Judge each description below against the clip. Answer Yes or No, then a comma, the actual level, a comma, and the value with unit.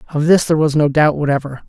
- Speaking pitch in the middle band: Yes, medium, 145 Hz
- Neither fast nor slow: No, fast, 250 wpm